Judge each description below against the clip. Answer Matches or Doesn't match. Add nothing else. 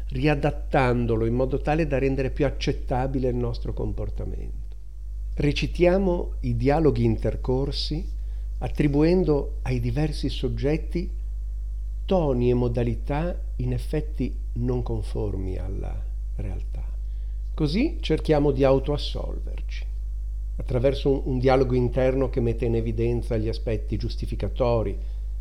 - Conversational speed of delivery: Doesn't match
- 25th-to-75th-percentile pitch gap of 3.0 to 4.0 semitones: Doesn't match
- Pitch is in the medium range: Doesn't match